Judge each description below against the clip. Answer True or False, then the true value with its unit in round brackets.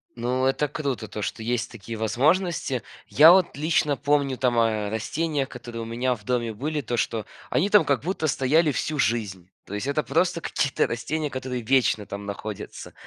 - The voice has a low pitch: True (130 Hz)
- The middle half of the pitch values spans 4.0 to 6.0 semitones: True (4.7 semitones)